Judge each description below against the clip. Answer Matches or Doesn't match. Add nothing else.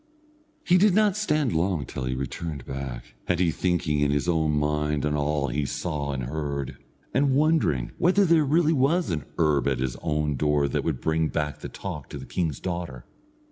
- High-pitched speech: Doesn't match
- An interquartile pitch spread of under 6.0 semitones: Doesn't match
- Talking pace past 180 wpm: Matches